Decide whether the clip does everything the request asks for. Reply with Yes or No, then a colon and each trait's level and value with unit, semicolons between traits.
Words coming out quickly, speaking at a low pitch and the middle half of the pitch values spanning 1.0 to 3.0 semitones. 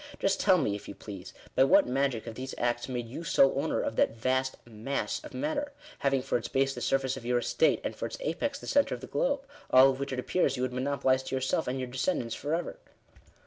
Yes: fast, 245 wpm; low, 130 Hz; narrow, 2.5 semitones